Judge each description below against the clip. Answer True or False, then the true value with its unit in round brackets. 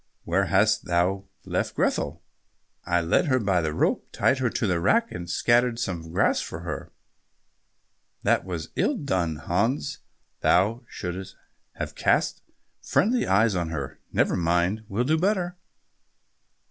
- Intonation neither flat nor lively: False (6.3 semitones)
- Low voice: True (95 Hz)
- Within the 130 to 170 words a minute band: True (145 wpm)